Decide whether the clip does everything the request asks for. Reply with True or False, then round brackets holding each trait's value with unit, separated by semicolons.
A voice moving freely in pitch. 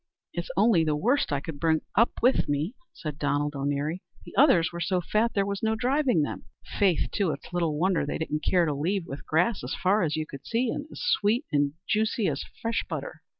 True (6.6 semitones)